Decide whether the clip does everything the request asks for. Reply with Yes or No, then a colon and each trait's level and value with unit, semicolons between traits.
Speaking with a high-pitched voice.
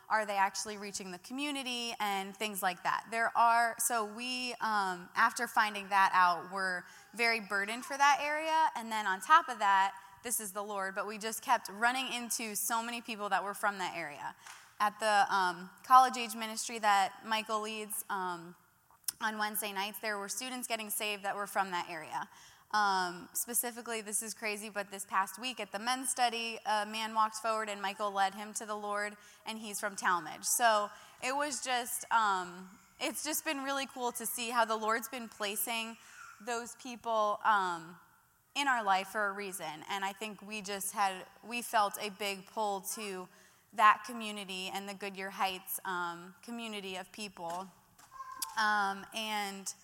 Yes: high, 215 Hz